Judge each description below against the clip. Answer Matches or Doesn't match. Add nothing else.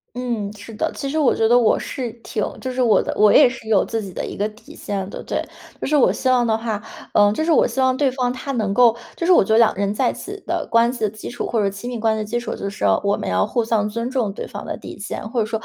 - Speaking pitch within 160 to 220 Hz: Doesn't match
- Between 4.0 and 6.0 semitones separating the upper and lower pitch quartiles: Doesn't match